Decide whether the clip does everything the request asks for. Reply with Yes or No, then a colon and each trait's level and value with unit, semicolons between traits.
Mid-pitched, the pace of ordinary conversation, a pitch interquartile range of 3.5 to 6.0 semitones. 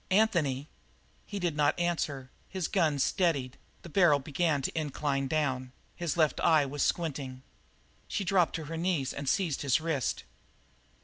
Yes: medium, 155 Hz; average, 150 wpm; average, 3.9 semitones